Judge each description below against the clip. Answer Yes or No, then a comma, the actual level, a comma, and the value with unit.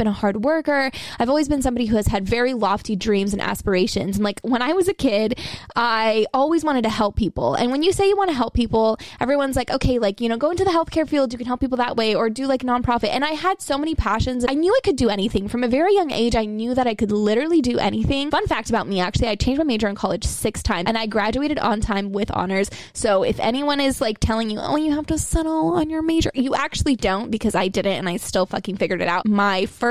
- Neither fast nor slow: No, fast, 275 wpm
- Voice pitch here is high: Yes, high, 240 Hz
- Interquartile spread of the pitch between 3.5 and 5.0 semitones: No, wide, 5.4 semitones